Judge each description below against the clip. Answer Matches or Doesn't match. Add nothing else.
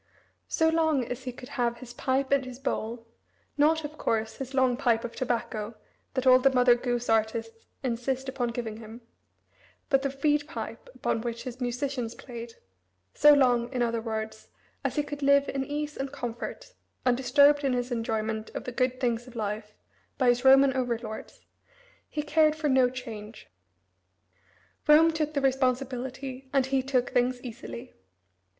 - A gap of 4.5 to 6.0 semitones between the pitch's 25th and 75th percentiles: Doesn't match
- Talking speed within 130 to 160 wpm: Doesn't match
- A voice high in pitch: Matches